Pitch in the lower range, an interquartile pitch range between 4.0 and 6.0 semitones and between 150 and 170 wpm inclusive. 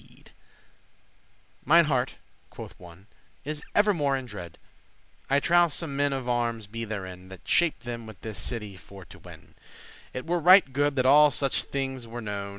No: low, 130 Hz; average, 5.3 semitones; average, 185 wpm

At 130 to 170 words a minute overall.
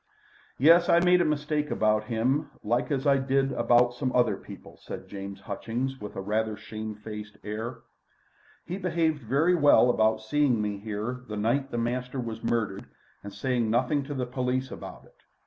No: average, 180 wpm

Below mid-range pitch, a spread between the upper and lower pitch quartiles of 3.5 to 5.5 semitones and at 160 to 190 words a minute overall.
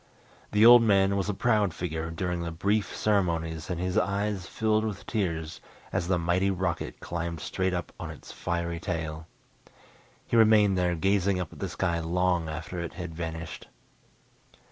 No: very low, 90 Hz; average, 3.0 semitones; average, 165 wpm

